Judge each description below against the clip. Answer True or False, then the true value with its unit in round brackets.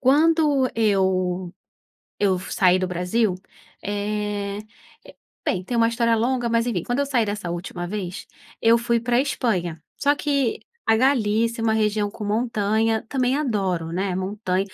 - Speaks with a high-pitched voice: True (215 Hz)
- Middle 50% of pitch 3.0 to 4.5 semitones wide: True (4.0 semitones)